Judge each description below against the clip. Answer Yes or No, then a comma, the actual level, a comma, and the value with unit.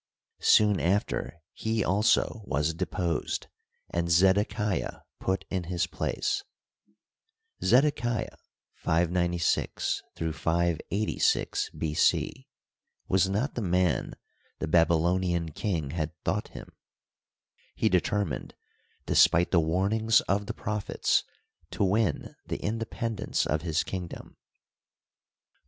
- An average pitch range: Yes, average, 3.8 semitones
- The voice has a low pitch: Yes, very low, 90 Hz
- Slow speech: Yes, slow, 100 wpm